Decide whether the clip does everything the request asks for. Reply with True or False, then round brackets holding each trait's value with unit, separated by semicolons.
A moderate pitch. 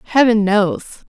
False (220 Hz)